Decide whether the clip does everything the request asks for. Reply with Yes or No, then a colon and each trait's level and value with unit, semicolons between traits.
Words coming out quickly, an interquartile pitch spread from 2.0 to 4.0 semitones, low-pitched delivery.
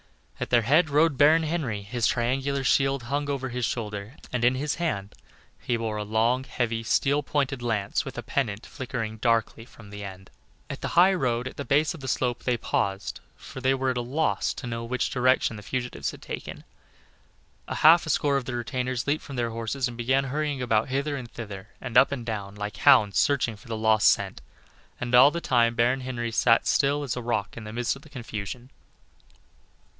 Yes: fast, 210 wpm; average, 3.3 semitones; low, 125 Hz